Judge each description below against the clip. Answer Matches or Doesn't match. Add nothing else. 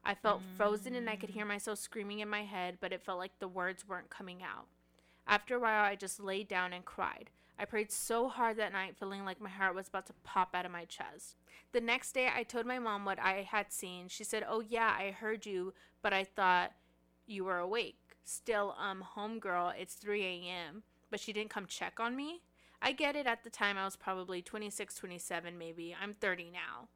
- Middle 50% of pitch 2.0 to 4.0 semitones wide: Matches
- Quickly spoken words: Matches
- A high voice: Matches